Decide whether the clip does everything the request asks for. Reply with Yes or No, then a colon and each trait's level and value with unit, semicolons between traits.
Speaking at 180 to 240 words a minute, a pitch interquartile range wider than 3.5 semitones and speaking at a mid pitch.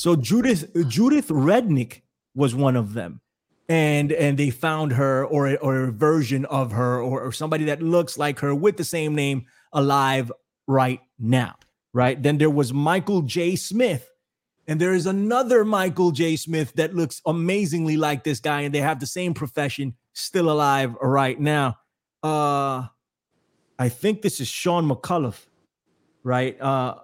No: average, 160 wpm; average, 4.0 semitones; medium, 145 Hz